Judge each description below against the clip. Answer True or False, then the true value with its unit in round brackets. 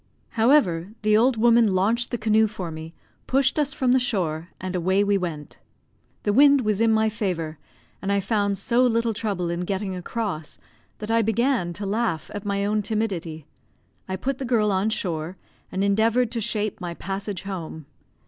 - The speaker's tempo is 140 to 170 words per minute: False (180 wpm)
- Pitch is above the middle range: True (205 Hz)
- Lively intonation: False (3.7 semitones)